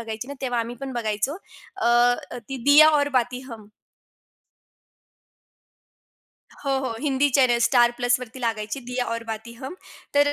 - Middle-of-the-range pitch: No, high, 245 Hz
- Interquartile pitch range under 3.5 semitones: Yes, average, 2.8 semitones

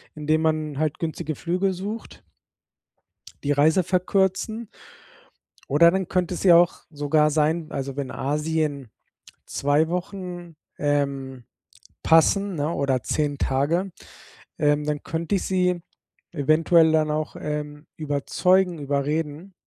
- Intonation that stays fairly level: No, average, 3.3 semitones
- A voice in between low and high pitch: Yes, medium, 155 Hz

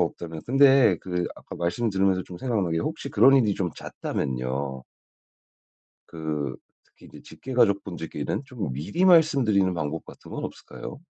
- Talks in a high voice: No, very low, 95 Hz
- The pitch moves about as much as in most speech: No, wide, 7.6 semitones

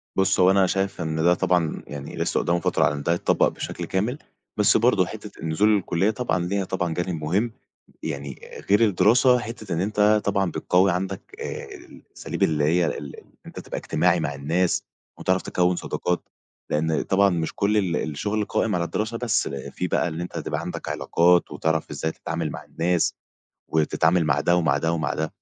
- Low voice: Yes, very low, 90 Hz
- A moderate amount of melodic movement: Yes, average, 3.5 semitones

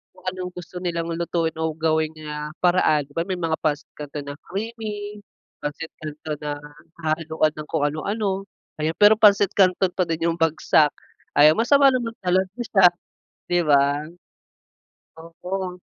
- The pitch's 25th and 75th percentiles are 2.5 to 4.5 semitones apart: Yes, average, 3.7 semitones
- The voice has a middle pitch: Yes, medium, 165 Hz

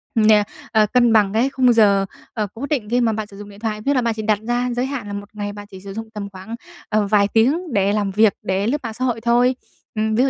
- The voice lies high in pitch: Yes, high, 220 Hz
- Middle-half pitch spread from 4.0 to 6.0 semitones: No, average, 2.8 semitones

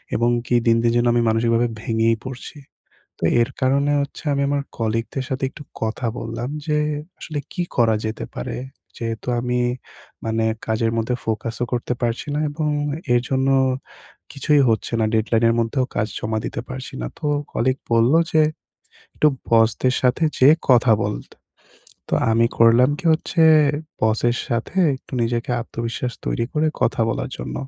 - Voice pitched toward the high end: No, low, 120 Hz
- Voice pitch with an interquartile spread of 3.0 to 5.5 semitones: No, narrow, 2.6 semitones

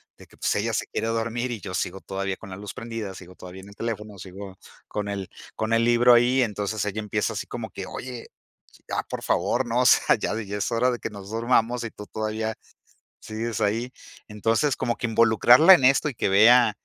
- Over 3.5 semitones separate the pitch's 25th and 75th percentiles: No, average, 2.7 semitones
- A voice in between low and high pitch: No, low, 110 Hz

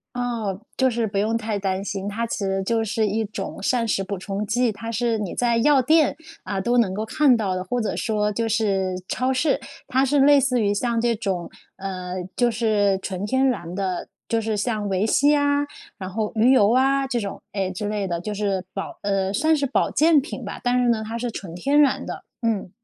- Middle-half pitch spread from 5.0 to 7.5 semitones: No, average, 3.8 semitones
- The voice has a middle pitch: No, high, 220 Hz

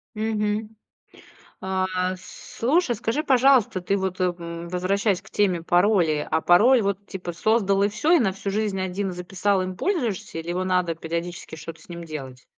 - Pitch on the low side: No, high, 190 Hz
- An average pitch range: Yes, average, 3.3 semitones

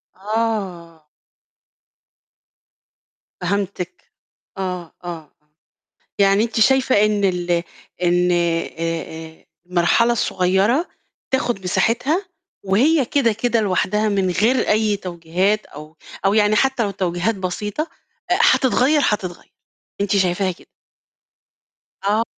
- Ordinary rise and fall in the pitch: Yes, average, 4.1 semitones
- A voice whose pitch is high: Yes, high, 195 Hz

